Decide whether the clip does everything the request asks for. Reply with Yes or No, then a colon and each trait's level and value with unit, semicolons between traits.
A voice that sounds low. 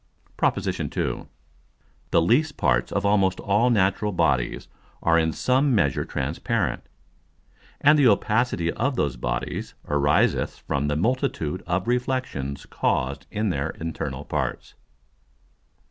Yes: very low, 95 Hz